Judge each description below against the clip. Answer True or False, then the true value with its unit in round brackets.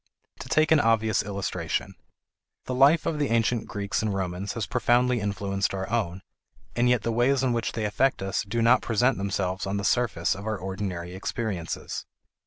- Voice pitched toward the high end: False (110 Hz)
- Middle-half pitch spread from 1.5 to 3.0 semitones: False (3.8 semitones)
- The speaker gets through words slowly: False (185 wpm)